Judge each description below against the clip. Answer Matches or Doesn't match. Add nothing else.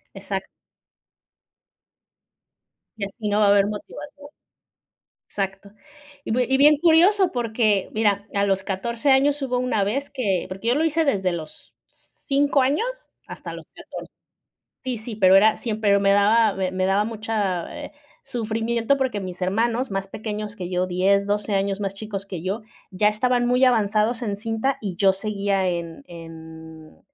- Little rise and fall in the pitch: Doesn't match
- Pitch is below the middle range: Doesn't match